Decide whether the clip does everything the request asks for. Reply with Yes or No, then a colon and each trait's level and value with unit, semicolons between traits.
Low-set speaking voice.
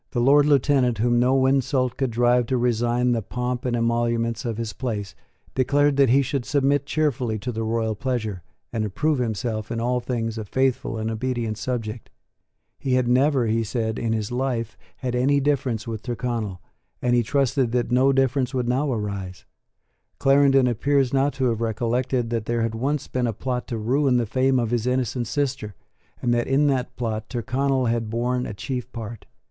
Yes: low, 125 Hz